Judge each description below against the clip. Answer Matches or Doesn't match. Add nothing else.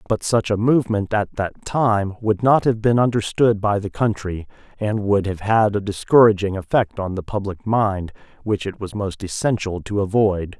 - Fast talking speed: Doesn't match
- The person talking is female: Doesn't match